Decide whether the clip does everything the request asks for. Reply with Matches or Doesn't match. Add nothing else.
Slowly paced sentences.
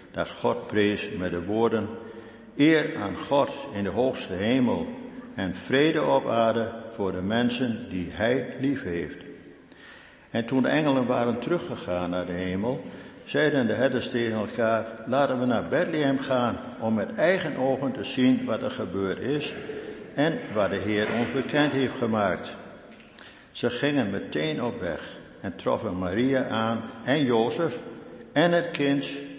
Doesn't match